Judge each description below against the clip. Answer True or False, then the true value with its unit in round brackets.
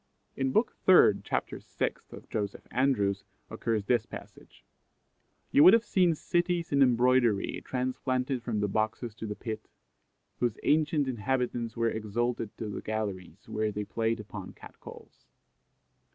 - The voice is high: False (115 Hz)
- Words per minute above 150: False (145 wpm)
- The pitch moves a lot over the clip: False (3.7 semitones)